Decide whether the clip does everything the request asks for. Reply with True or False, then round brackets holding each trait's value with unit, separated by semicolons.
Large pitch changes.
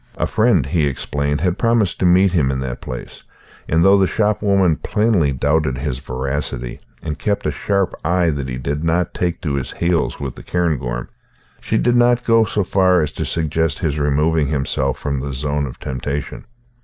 False (4.9 semitones)